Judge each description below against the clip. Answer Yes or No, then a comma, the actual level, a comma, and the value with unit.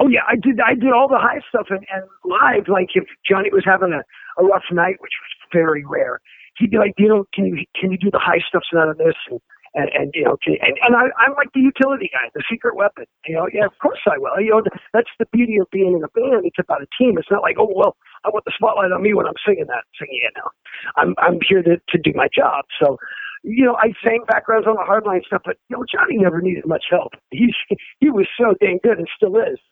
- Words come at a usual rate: No, fast, 270 wpm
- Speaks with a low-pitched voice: No, high, 220 Hz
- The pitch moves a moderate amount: No, wide, 5.7 semitones